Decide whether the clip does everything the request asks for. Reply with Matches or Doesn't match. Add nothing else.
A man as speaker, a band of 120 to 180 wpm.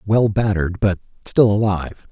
Matches